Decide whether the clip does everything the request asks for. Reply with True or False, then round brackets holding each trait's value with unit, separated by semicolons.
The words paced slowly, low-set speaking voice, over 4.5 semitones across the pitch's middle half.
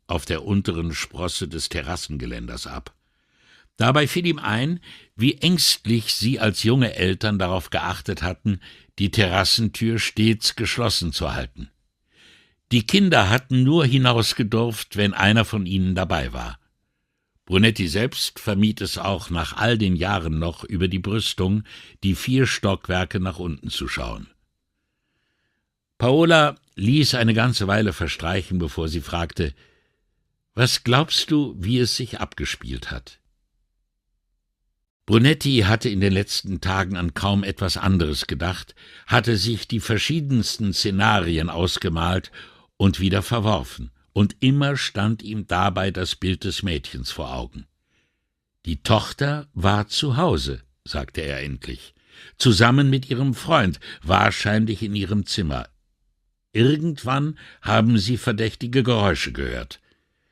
True (125 wpm; 100 Hz; 5.0 semitones)